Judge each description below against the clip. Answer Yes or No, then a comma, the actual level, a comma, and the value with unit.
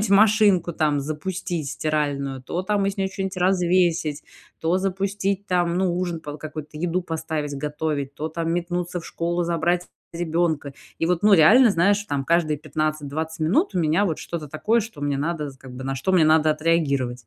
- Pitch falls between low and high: Yes, medium, 165 Hz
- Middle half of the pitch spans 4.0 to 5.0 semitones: No, average, 3.3 semitones